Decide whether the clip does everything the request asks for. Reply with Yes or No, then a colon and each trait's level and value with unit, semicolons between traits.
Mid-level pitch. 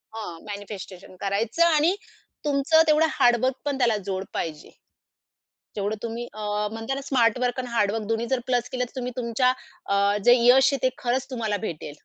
No: high, 240 Hz